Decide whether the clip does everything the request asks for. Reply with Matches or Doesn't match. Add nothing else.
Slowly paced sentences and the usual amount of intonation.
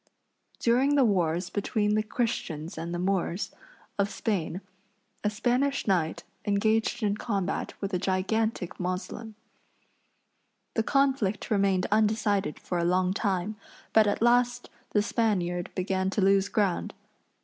Matches